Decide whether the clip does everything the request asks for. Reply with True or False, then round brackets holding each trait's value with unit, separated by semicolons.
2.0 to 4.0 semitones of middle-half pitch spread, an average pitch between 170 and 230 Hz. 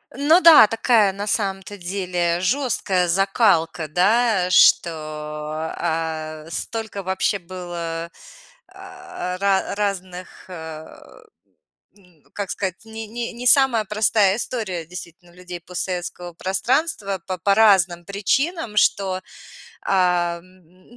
True (3.6 semitones; 190 Hz)